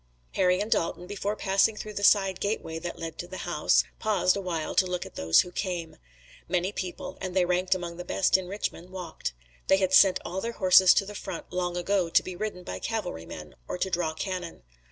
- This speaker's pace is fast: Yes, fast, 215 wpm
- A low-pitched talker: No, medium, 185 Hz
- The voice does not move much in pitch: Yes, narrow, 1.8 semitones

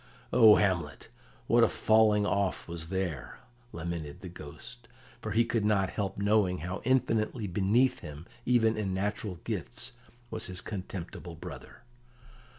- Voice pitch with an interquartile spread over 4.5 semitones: No, average, 4.0 semitones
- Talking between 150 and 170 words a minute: No, average, 140 wpm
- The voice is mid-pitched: No, low, 100 Hz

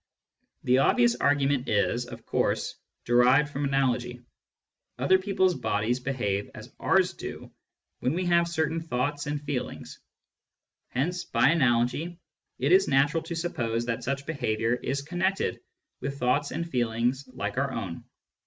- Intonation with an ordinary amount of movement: Yes, average, 4.7 semitones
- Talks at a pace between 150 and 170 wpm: No, average, 140 wpm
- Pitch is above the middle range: No, low, 135 Hz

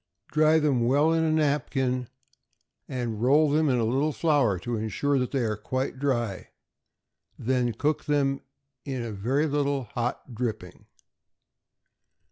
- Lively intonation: No, average, 3.6 semitones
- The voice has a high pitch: No, low, 130 Hz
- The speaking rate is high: No, average, 140 wpm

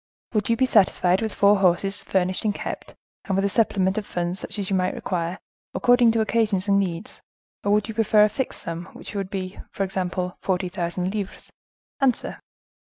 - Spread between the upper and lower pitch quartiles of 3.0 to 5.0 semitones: No, narrow, 2.6 semitones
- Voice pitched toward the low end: No, high, 195 Hz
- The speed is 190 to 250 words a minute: Yes, average, 195 wpm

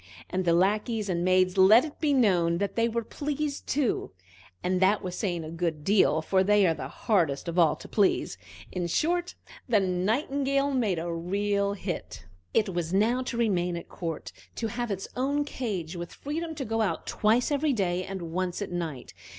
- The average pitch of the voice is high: Yes, high, 195 Hz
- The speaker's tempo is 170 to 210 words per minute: Yes, average, 190 wpm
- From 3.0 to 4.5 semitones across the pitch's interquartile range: No, average, 5.3 semitones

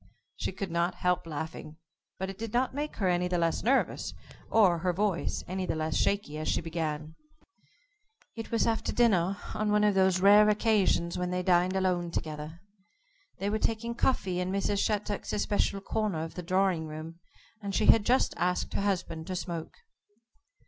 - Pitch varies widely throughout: No, average, 3.5 semitones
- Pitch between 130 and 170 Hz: No, medium, 185 Hz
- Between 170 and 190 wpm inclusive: Yes, average, 180 wpm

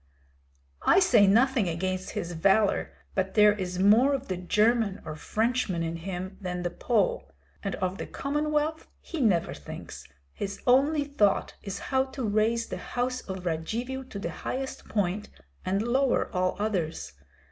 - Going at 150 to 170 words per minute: Yes, average, 160 wpm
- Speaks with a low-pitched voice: No, high, 210 Hz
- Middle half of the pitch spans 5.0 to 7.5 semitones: Yes, wide, 5.5 semitones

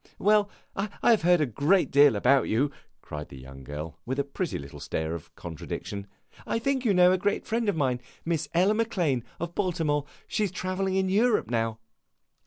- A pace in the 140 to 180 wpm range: No, average, 195 wpm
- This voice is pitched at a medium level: Yes, medium, 160 Hz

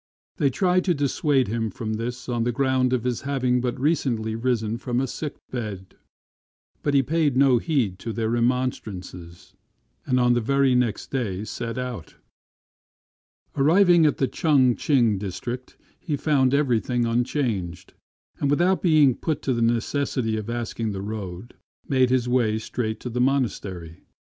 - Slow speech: No, average, 160 wpm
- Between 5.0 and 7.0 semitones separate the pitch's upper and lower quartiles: No, average, 3.6 semitones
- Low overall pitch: Yes, low, 125 Hz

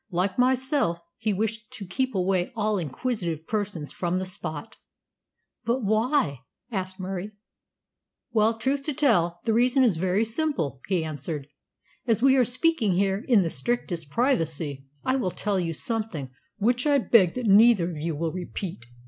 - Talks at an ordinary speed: Yes, average, 160 wpm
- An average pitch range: No, wide, 5.9 semitones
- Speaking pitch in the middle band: No, high, 200 Hz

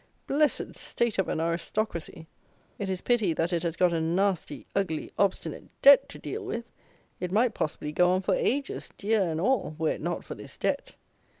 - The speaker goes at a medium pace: Yes, average, 190 wpm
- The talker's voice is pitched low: No, medium, 185 Hz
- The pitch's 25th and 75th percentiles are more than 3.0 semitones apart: Yes, average, 5.0 semitones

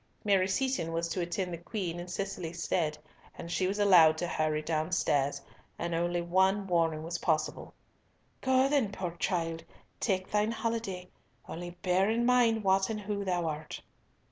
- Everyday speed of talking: Yes, average, 165 wpm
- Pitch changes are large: No, average, 3.3 semitones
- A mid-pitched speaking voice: Yes, medium, 180 Hz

